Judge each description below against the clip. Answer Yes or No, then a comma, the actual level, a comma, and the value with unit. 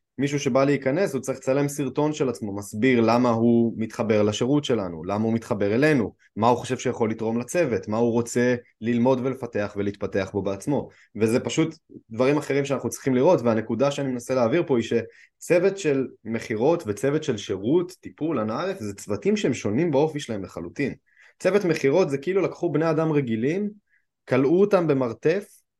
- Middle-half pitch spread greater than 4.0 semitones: Yes, average, 4.4 semitones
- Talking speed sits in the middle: No, fast, 165 wpm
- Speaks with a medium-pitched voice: No, low, 130 Hz